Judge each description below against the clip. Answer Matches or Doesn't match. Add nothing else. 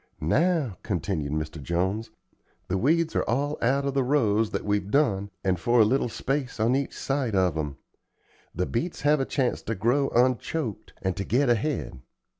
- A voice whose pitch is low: Matches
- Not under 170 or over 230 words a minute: Matches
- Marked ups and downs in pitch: Matches